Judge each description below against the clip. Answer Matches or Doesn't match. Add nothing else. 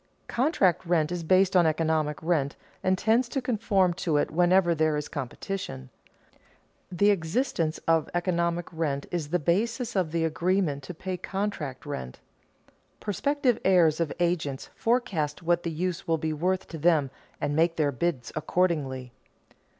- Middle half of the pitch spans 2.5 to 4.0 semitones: Matches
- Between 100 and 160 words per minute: Matches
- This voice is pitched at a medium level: Matches